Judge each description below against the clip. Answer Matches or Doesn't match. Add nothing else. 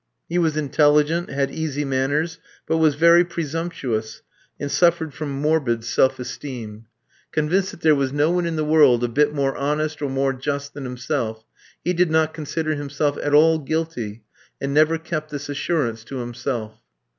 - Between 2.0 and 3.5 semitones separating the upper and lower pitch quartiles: Matches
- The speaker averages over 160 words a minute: Matches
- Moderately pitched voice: Matches